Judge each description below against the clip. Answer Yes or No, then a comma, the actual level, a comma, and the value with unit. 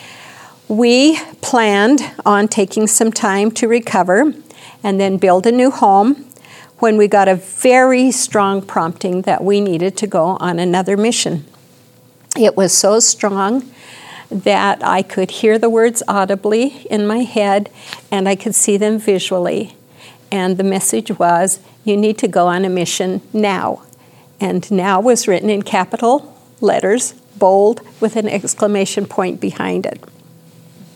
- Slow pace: No, average, 145 wpm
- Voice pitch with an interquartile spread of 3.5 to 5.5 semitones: No, average, 3.1 semitones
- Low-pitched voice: No, high, 200 Hz